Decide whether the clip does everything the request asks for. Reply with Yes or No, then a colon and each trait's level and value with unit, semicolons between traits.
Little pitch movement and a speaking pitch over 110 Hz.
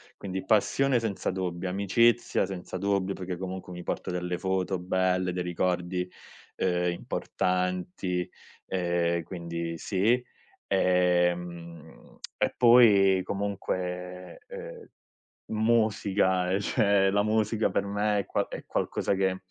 No: narrow, 2.2 semitones; very low, 95 Hz